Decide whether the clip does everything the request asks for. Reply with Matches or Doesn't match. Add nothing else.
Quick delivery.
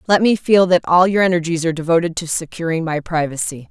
Matches